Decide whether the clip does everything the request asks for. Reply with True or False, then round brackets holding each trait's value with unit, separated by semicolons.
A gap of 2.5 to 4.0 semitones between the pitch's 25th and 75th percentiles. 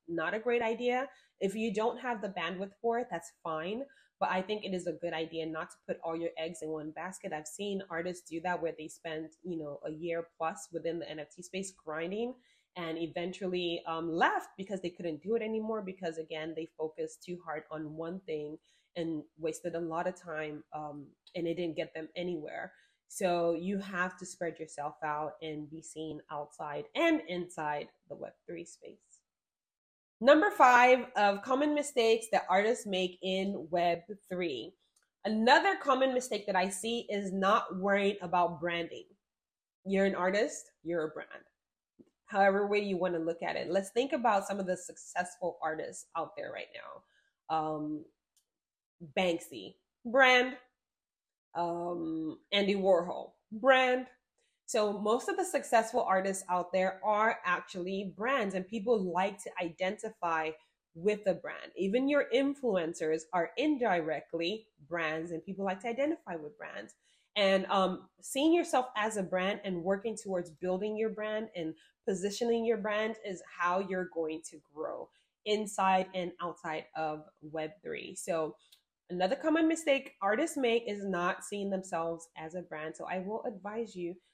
False (4.7 semitones)